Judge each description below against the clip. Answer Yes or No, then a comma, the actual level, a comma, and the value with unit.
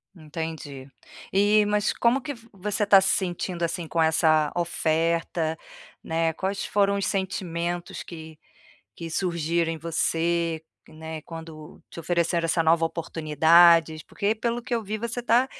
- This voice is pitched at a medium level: Yes, medium, 170 Hz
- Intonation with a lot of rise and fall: No, average, 3.5 semitones